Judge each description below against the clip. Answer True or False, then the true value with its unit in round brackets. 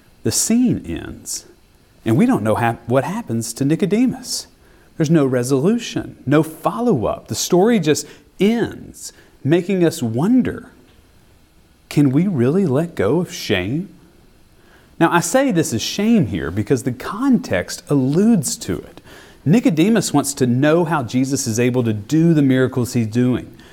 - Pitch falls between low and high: True (150 Hz)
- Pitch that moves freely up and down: True (6.7 semitones)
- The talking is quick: False (145 wpm)